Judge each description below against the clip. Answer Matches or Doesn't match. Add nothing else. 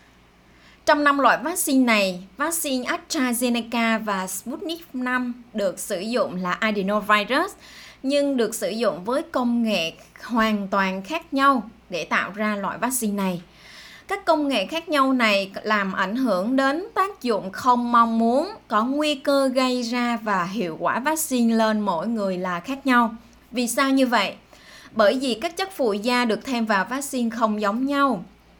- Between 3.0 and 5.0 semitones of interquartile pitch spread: Matches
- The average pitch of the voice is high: Matches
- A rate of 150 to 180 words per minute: Matches